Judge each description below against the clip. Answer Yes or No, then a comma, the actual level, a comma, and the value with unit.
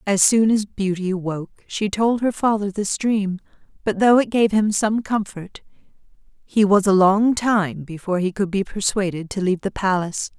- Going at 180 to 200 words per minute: Yes, average, 185 wpm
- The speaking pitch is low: No, high, 200 Hz